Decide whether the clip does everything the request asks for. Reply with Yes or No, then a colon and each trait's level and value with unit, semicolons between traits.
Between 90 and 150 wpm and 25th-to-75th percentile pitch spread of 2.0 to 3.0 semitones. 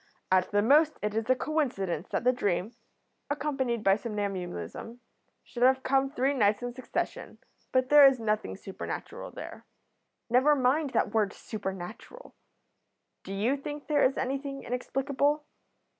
No: average, 145 wpm; average, 5.0 semitones